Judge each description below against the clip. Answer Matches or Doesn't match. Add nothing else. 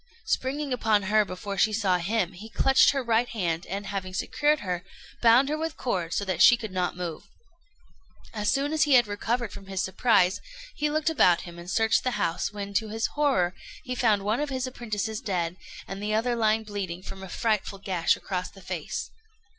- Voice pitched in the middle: Doesn't match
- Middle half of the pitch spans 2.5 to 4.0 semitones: Doesn't match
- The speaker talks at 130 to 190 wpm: Doesn't match